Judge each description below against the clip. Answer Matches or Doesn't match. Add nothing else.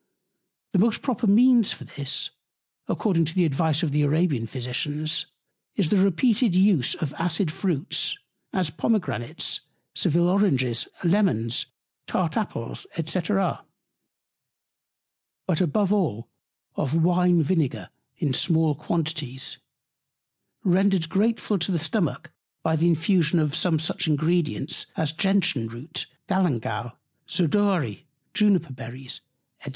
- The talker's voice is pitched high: Doesn't match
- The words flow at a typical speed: Doesn't match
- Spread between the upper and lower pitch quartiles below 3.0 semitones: Doesn't match